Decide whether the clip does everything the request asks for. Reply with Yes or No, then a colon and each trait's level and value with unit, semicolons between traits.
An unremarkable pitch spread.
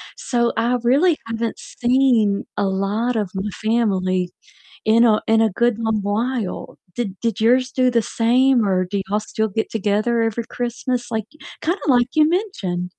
Yes: average, 3.0 semitones